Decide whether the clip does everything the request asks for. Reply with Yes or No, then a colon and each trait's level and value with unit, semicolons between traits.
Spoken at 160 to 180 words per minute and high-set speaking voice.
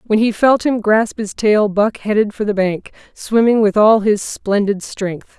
No: average, 200 wpm; high, 210 Hz